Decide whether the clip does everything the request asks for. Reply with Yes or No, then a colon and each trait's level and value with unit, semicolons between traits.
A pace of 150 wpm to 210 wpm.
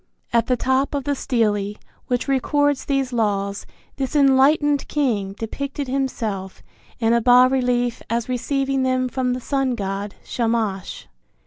No: average, 140 wpm